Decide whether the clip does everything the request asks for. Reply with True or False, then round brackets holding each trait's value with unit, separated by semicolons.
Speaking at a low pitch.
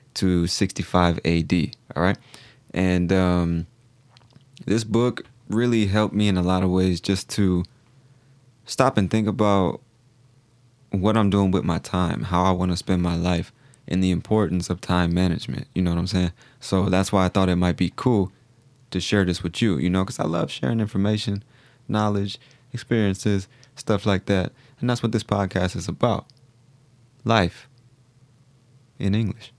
True (105 Hz)